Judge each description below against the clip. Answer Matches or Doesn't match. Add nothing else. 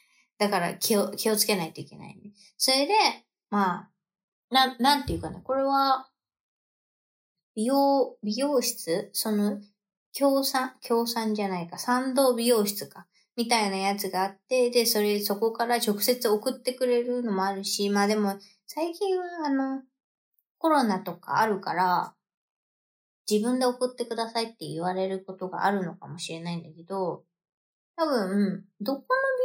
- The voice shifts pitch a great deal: Doesn't match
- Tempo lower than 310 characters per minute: Matches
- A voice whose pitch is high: Matches